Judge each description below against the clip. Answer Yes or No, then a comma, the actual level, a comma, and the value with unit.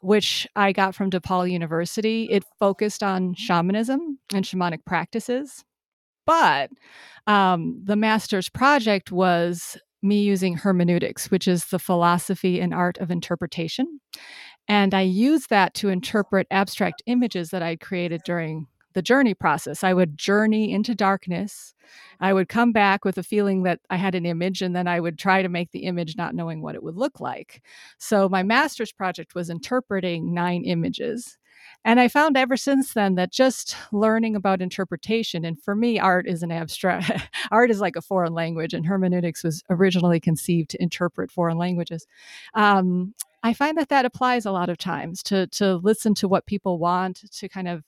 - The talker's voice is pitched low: No, high, 190 Hz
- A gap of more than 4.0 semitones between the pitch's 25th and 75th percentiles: No, average, 3.7 semitones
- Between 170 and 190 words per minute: Yes, average, 175 wpm